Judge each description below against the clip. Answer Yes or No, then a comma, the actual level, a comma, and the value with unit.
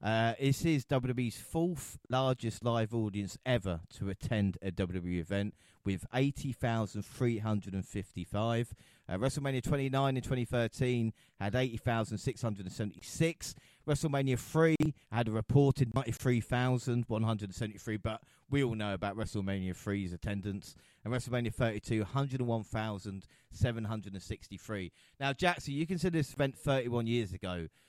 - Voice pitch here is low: Yes, low, 115 Hz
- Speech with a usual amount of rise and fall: Yes, average, 4.4 semitones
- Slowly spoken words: Yes, slow, 110 wpm